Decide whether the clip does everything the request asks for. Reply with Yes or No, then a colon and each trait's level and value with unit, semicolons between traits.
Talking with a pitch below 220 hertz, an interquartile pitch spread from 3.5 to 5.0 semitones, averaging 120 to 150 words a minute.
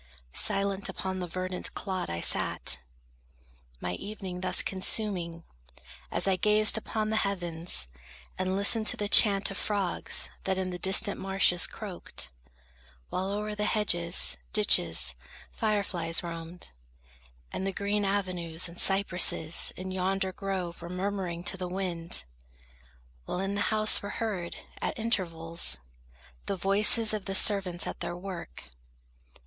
No: high, 190 Hz; narrow, 2.6 semitones; average, 140 wpm